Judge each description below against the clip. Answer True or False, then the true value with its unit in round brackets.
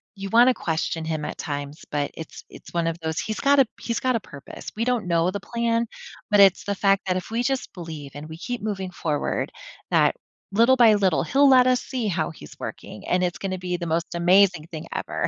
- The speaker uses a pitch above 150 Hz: True (185 Hz)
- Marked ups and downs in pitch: True (6.0 semitones)